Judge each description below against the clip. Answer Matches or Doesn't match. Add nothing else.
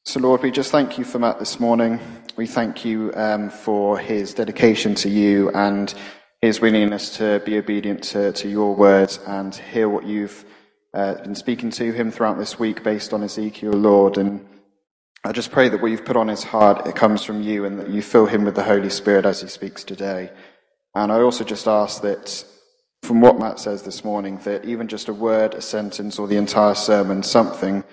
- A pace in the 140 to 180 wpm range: Doesn't match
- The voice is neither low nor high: Doesn't match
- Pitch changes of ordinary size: Doesn't match